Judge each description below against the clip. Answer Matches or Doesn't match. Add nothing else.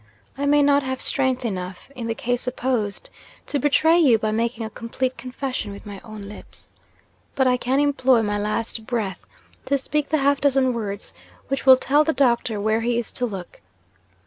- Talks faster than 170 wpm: Matches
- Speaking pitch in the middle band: Doesn't match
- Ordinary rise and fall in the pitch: Matches